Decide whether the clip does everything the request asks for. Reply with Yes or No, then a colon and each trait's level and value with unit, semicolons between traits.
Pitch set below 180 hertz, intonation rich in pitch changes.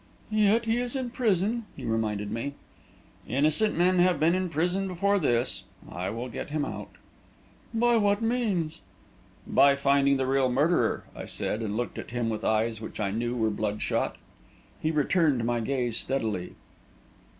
Yes: medium, 140 Hz; wide, 8.7 semitones